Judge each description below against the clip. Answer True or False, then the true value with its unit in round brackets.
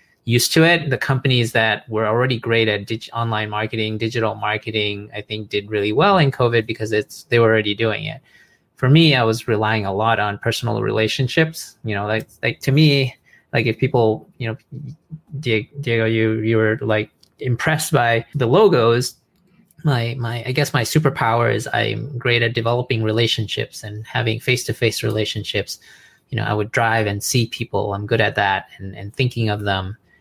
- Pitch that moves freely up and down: False (3.1 semitones)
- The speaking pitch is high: False (115 Hz)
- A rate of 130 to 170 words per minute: False (185 wpm)